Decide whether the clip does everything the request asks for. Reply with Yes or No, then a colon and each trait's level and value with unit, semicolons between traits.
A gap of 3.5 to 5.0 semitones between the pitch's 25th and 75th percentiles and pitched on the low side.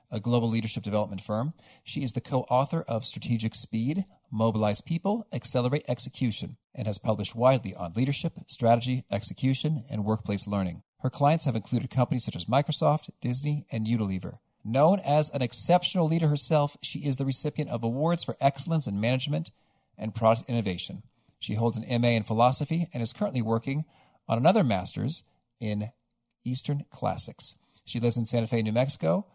Yes: average, 4.5 semitones; low, 125 Hz